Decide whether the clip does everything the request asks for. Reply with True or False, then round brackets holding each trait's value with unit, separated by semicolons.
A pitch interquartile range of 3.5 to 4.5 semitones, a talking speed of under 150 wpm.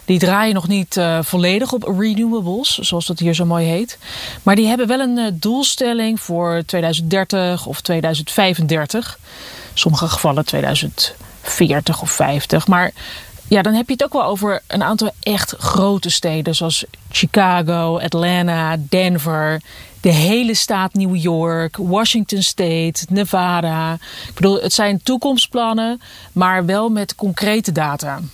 True (4.0 semitones; 140 wpm)